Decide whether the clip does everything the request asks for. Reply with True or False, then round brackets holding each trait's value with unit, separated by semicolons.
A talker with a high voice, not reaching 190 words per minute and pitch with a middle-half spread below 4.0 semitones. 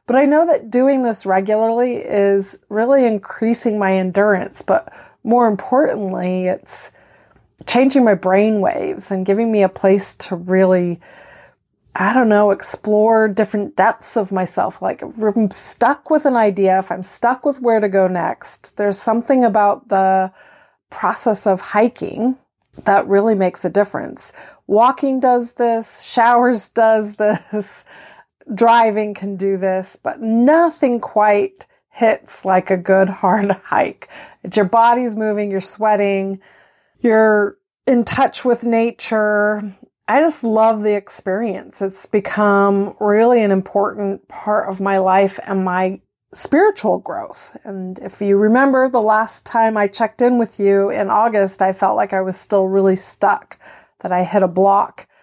True (210 Hz; 150 wpm; 3.1 semitones)